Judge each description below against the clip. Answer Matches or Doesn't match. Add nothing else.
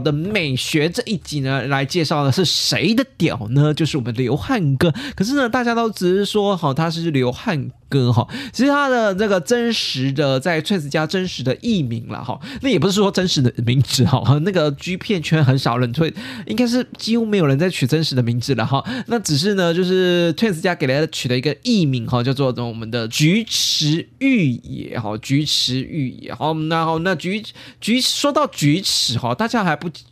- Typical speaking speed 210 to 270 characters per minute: Doesn't match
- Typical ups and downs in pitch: Doesn't match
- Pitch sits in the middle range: Matches